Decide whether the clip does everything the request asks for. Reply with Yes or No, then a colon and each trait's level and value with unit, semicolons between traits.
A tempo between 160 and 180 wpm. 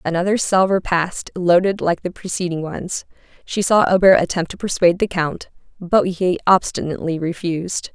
No: average, 150 wpm